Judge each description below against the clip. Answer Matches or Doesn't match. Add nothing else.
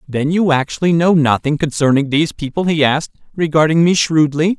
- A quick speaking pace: Doesn't match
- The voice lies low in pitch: Doesn't match